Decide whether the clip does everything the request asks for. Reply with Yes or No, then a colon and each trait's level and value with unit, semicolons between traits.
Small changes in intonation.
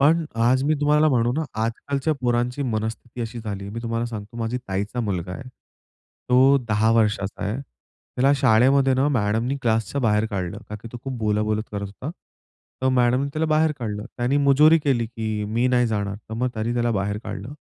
No: average, 3.6 semitones